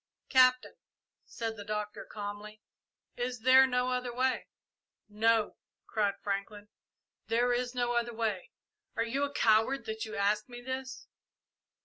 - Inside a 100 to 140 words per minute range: Yes, slow, 135 wpm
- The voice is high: Yes, high, 230 Hz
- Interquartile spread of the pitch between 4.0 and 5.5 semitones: No, average, 3.0 semitones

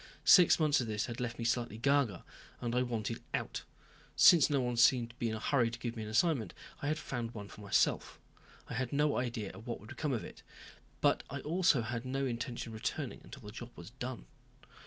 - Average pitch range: Yes, average, 3.2 semitones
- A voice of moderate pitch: No, low, 120 Hz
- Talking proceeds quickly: Yes, fast, 225 wpm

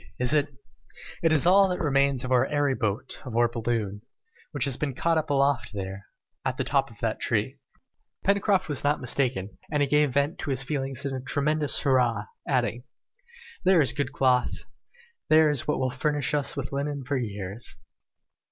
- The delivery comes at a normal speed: Yes, average, 190 wpm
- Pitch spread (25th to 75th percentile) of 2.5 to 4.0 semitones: Yes, average, 3.2 semitones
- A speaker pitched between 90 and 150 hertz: Yes, medium, 140 Hz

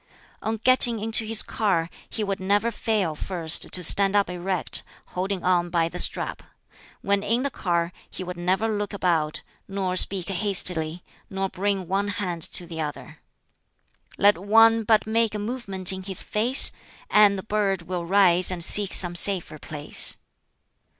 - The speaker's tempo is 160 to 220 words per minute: Yes, average, 165 wpm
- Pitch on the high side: Yes, high, 195 Hz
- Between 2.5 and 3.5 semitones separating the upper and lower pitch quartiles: Yes, average, 2.9 semitones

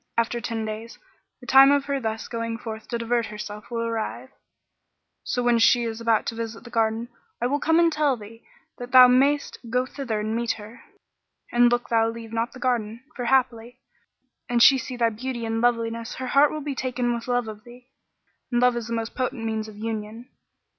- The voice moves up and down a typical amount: No, narrow, 1.8 semitones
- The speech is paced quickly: Yes, fast, 210 wpm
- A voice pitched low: No, high, 235 Hz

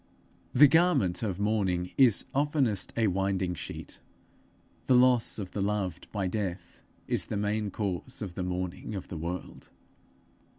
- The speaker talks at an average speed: Yes, average, 145 wpm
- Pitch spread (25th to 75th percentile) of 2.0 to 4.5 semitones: Yes, average, 3.5 semitones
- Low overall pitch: Yes, low, 100 Hz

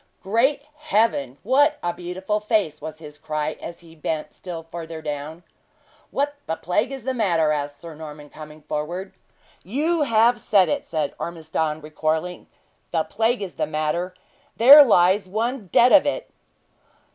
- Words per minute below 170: Yes, average, 155 wpm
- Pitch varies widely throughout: Yes, wide, 6.7 semitones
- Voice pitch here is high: No, medium, 175 Hz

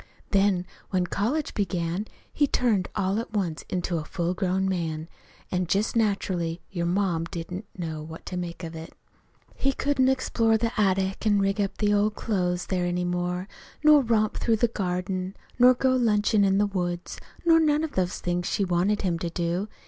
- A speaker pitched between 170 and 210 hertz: Yes, high, 190 Hz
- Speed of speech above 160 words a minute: Yes, average, 185 wpm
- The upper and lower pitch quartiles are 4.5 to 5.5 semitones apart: No, average, 3.4 semitones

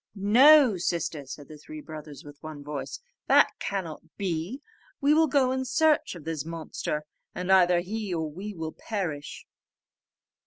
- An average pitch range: No, wide, 8.2 semitones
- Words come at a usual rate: Yes, average, 155 wpm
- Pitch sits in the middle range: Yes, medium, 175 Hz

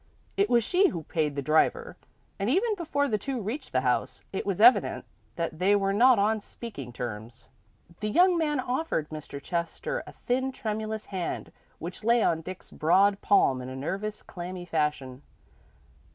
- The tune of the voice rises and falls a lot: Yes, wide, 8.0 semitones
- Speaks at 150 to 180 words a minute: Yes, average, 170 wpm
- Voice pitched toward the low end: No, high, 200 Hz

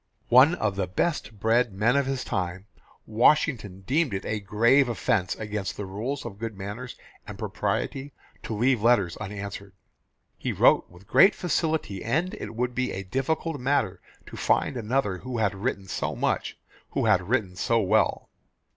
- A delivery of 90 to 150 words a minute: No, average, 165 wpm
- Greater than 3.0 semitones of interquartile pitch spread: Yes, average, 4.8 semitones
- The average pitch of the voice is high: No, low, 110 Hz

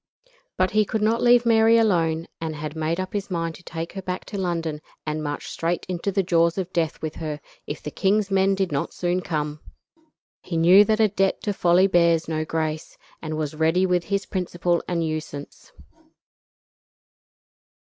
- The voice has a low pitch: No, medium, 175 Hz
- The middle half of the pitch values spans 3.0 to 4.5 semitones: Yes, average, 3.3 semitones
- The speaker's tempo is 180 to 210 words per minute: Yes, average, 185 wpm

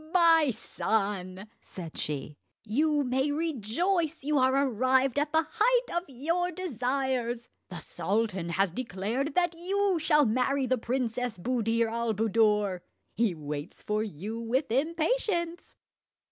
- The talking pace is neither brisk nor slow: No, slow, 130 wpm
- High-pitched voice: Yes, very high, 255 Hz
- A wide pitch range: Yes, wide, 6.6 semitones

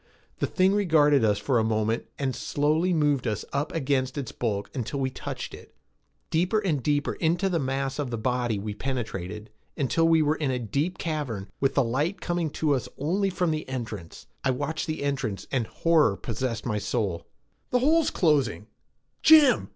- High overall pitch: No, medium, 140 Hz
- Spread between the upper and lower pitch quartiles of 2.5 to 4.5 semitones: No, wide, 5.5 semitones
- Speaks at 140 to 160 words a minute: No, average, 180 wpm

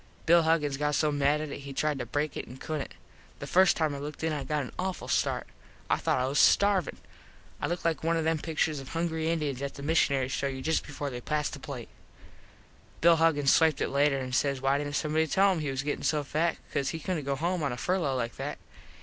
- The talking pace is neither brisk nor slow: No, fast, 250 wpm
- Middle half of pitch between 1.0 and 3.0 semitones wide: Yes, average, 2.7 semitones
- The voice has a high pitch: No, medium, 150 Hz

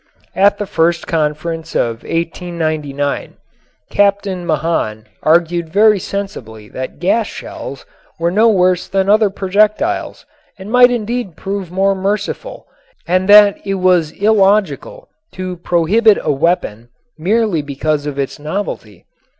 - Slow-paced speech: Yes, slow, 125 wpm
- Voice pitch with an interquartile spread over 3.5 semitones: Yes, average, 4.4 semitones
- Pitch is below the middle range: No, medium, 185 Hz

